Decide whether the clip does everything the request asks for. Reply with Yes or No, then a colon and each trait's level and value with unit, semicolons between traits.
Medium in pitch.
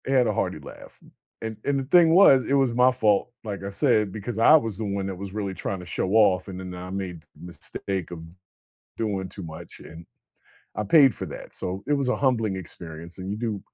No: low, 100 Hz